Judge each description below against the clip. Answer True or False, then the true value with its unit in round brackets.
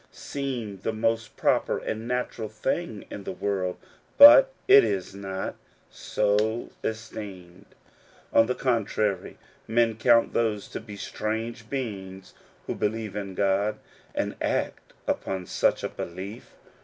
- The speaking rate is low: True (130 wpm)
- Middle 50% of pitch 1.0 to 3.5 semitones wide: True (2.7 semitones)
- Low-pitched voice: True (110 Hz)